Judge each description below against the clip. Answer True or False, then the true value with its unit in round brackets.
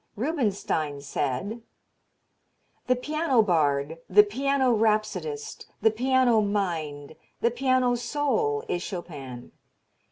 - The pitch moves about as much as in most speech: False (7.7 semitones)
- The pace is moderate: False (95 wpm)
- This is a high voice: True (215 Hz)